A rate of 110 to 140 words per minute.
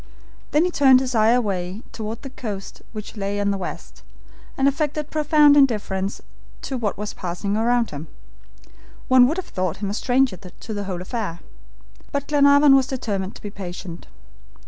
No: average, 170 wpm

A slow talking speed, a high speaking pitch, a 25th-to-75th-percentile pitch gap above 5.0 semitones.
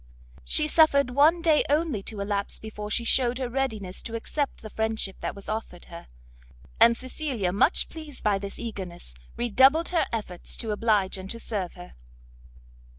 No: average, 165 wpm; high, 225 Hz; wide, 5.5 semitones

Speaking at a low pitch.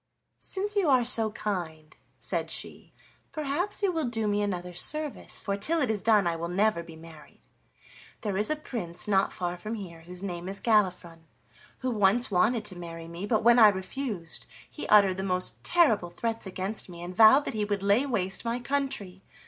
No: high, 205 Hz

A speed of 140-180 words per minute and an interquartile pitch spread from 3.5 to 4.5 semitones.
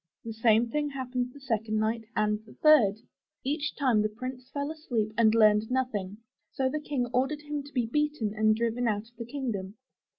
No: average, 195 wpm; average, 4.1 semitones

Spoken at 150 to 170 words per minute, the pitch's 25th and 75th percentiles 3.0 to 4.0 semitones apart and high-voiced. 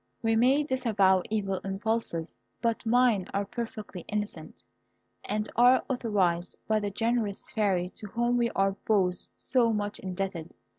No: average, 140 wpm; average, 3.3 semitones; high, 210 Hz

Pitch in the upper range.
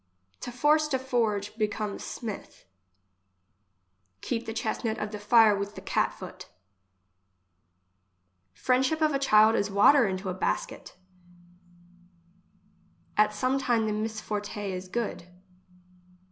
Yes: high, 220 Hz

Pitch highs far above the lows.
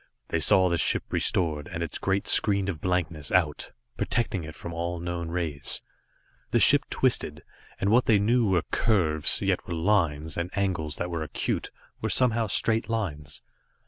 No: average, 4.0 semitones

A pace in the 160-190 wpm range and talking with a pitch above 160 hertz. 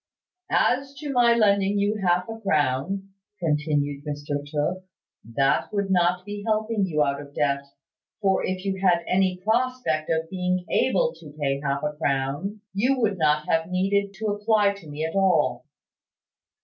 Yes: average, 165 wpm; medium, 185 Hz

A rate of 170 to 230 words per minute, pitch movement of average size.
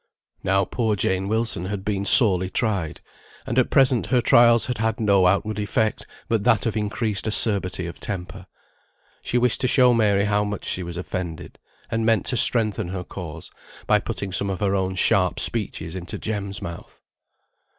Yes: average, 175 wpm; average, 3.2 semitones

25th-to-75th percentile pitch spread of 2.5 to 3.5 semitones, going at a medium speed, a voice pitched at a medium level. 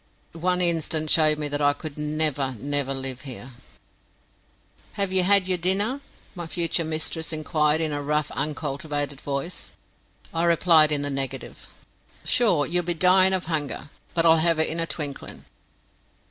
Yes: average, 3.0 semitones; average, 160 wpm; medium, 155 Hz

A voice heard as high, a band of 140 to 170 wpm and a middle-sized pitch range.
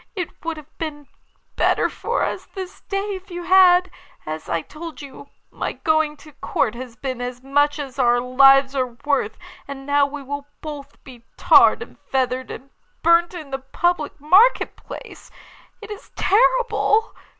Yes: very high, 290 Hz; average, 165 wpm; average, 4.7 semitones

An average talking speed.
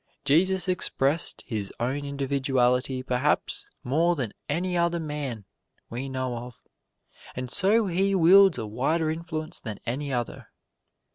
No: slow, 130 wpm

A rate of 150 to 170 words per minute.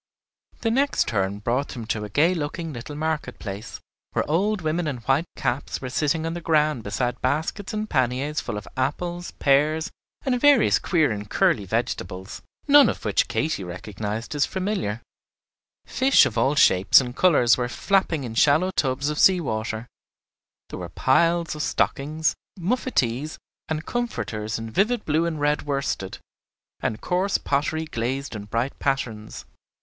Yes: average, 160 wpm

